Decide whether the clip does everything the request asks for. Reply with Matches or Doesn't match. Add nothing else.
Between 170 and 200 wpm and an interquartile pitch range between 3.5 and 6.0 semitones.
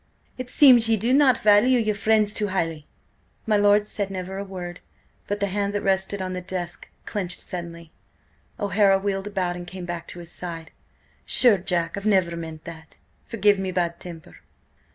Doesn't match